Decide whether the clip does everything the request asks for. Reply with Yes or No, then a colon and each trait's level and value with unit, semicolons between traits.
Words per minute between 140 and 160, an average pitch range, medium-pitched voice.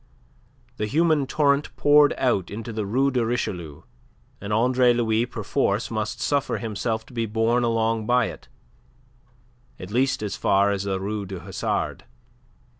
No: average, 150 wpm; average, 3.4 semitones; low, 115 Hz